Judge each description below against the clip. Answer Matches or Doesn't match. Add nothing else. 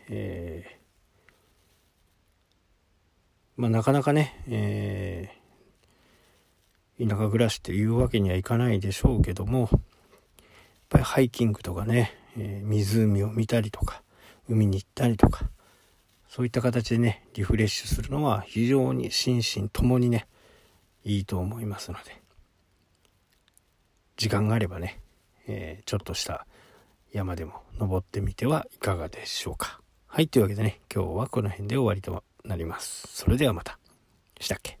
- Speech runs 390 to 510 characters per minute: Doesn't match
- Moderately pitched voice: Doesn't match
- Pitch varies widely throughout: Doesn't match